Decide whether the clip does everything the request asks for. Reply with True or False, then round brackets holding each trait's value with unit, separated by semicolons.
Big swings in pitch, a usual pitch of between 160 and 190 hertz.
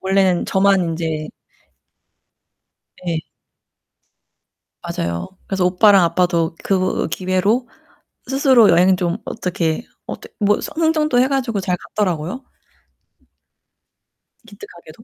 False (3.9 semitones; 185 Hz)